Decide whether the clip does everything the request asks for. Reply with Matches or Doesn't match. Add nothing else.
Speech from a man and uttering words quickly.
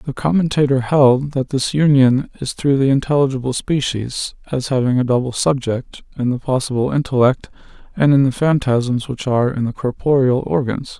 Doesn't match